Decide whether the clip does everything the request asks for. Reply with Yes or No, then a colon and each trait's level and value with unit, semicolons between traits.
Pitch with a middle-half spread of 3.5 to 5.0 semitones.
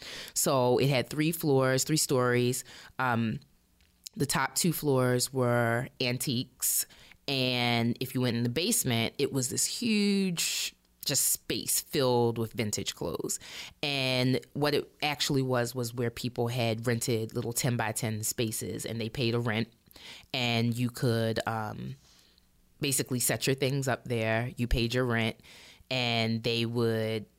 No: narrow, 2.4 semitones